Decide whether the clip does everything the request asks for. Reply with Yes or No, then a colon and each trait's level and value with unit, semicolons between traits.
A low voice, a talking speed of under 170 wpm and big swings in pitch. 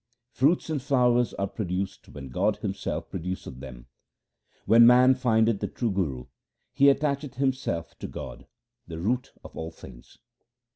Yes: low, 110 Hz; average, 145 wpm; wide, 7.1 semitones